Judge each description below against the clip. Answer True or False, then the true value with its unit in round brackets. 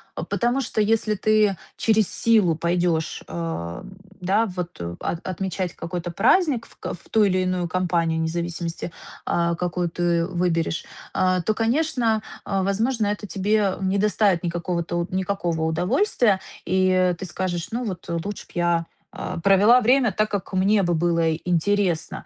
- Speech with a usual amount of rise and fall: True (3.6 semitones)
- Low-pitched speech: False (185 Hz)